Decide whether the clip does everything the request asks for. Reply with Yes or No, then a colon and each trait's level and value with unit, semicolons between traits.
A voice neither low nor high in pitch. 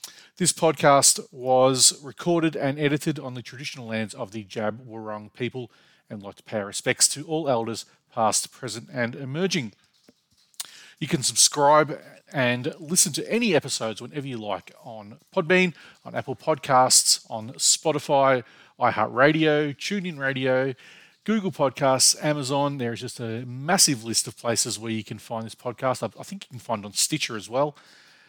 No: low, 130 Hz